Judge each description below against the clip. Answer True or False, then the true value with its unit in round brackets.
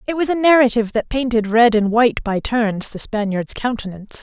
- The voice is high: True (230 Hz)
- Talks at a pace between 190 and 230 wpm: True (200 wpm)